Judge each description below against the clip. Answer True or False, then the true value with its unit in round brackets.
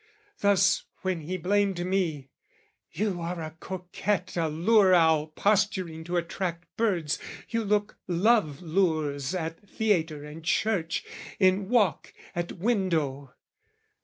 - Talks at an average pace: False (120 wpm)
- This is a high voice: False (180 Hz)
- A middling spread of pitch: True (3.7 semitones)